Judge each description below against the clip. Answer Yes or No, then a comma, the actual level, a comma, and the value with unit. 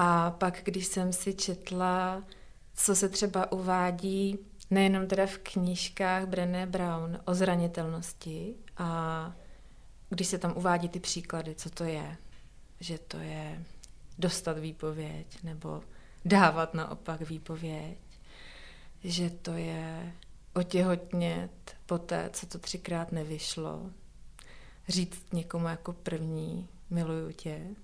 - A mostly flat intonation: Yes, narrow, 2.3 semitones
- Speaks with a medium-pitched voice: Yes, medium, 175 Hz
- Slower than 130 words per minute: Yes, slow, 115 wpm